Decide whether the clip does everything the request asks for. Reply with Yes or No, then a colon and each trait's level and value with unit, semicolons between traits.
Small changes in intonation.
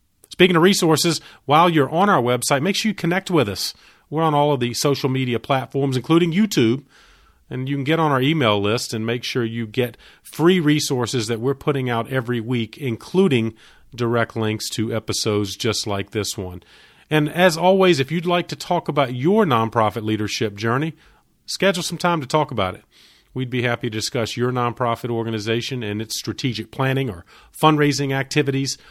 No: wide, 5.4 semitones